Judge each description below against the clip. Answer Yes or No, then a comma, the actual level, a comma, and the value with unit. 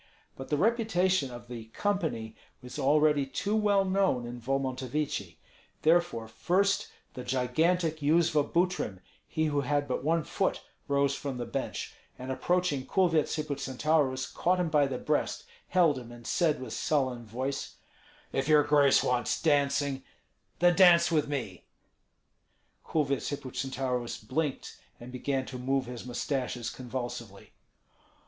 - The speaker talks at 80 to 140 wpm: Yes, slow, 135 wpm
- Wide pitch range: No, average, 4.2 semitones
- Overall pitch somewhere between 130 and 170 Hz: Yes, medium, 140 Hz